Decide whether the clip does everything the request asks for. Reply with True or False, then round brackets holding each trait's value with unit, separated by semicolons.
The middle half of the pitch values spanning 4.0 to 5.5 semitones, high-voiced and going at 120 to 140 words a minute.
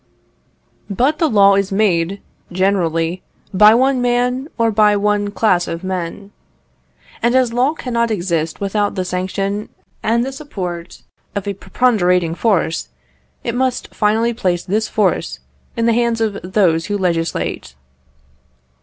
True (4.3 semitones; 205 Hz; 135 wpm)